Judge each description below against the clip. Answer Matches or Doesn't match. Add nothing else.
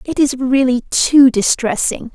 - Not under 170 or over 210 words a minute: Doesn't match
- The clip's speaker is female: Matches